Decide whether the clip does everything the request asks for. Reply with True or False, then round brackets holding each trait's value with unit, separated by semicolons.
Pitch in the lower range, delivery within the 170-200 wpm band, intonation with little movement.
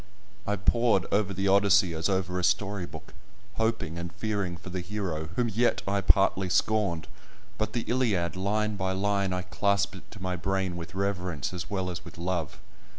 True (95 Hz; 180 wpm; 2.3 semitones)